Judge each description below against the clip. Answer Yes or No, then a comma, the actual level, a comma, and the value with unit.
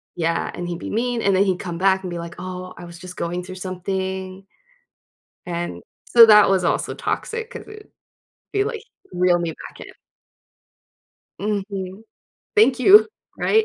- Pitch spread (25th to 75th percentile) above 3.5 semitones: No, average, 3.2 semitones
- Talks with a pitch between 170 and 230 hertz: Yes, high, 190 Hz